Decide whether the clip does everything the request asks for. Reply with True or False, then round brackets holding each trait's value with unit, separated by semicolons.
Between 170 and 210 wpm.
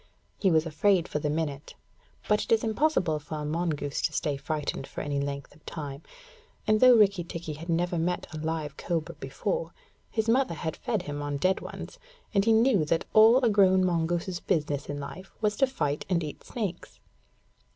True (195 wpm)